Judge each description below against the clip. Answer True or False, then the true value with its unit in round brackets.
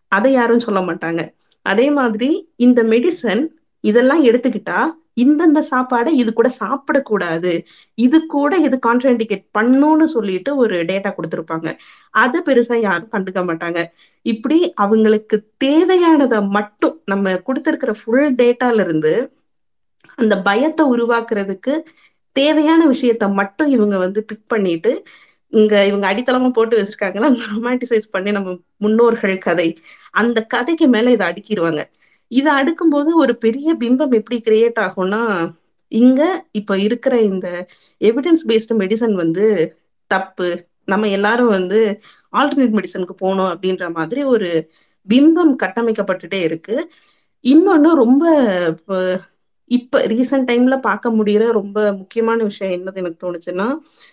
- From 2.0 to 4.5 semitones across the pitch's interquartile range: False (5.3 semitones)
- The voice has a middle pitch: False (225 Hz)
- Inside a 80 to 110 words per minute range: False (120 wpm)